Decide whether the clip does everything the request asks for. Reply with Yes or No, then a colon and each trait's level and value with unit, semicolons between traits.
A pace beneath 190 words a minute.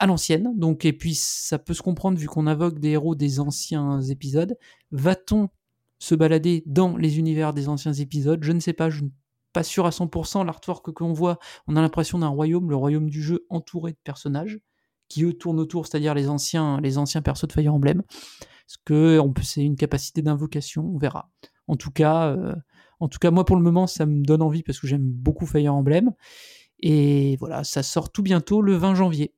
No: average, 215 wpm